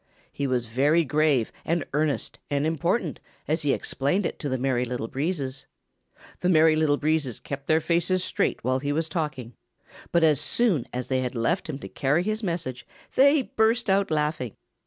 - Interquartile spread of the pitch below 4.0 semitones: No, average, 4.3 semitones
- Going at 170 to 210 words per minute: Yes, average, 180 wpm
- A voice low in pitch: No, medium, 150 Hz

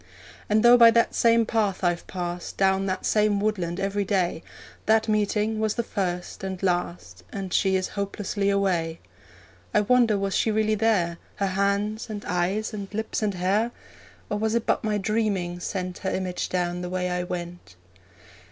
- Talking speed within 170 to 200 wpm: Yes, average, 175 wpm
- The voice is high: Yes, high, 200 Hz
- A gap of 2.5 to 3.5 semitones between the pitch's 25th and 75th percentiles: Yes, average, 3.0 semitones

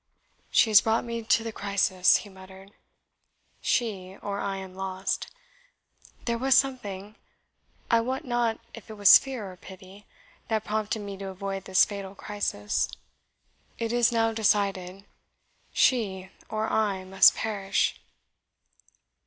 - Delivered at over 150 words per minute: No, slow, 135 wpm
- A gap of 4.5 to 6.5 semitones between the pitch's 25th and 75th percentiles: No, average, 2.8 semitones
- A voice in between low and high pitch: No, high, 205 Hz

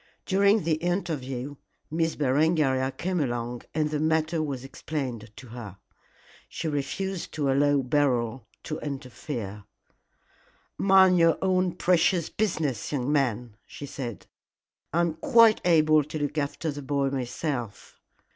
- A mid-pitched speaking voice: Yes, medium, 145 Hz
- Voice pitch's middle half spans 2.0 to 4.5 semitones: Yes, average, 4.1 semitones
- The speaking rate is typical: No, slow, 130 wpm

